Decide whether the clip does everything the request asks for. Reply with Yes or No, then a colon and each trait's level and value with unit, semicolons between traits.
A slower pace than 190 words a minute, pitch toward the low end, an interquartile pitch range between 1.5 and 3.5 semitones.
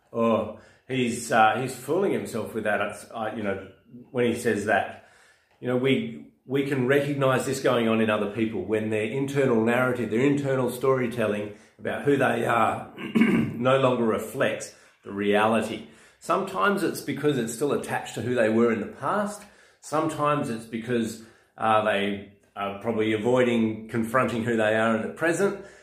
Yes: average, 165 wpm; low, 115 Hz; average, 3.1 semitones